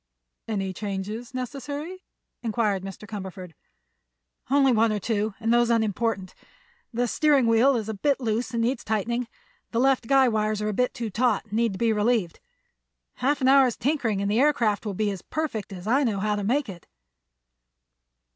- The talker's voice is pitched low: No, high, 225 Hz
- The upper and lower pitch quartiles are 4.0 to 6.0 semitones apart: No, average, 3.3 semitones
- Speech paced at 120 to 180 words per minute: Yes, average, 175 wpm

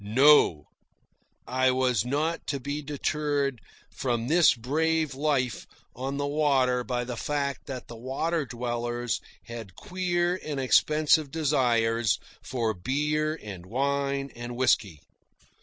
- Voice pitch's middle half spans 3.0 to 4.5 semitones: Yes, average, 3.8 semitones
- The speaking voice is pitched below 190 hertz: Yes, low, 135 Hz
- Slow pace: Yes, slow, 125 wpm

